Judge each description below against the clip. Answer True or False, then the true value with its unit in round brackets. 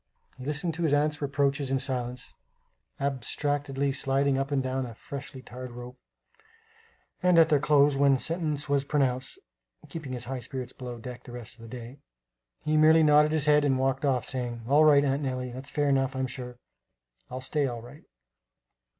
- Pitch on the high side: False (135 Hz)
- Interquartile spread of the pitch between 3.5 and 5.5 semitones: False (2.5 semitones)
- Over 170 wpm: True (185 wpm)